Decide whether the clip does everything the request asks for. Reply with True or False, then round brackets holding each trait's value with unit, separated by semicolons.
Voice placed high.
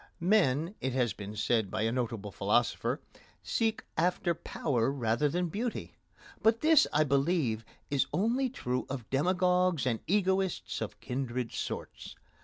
False (140 Hz)